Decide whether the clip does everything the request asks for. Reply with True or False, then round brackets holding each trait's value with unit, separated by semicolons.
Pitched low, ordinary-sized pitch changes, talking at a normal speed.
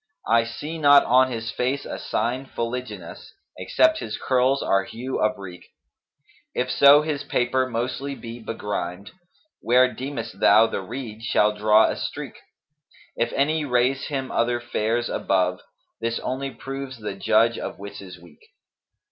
True (120 Hz; 3.7 semitones; 165 wpm)